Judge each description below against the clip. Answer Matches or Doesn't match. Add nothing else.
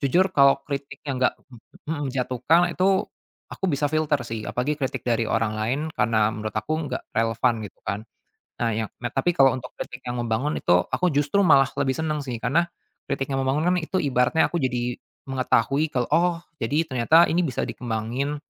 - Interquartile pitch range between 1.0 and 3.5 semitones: Doesn't match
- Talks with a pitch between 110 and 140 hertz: Matches